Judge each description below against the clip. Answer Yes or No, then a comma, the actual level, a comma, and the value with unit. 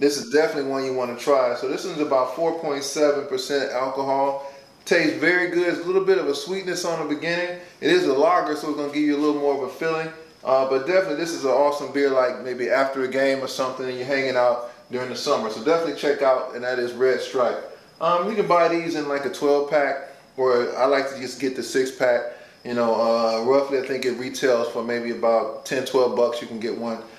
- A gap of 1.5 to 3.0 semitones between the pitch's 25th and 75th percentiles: No, average, 3.7 semitones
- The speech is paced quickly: Yes, fast, 245 wpm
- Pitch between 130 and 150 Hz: Yes, medium, 140 Hz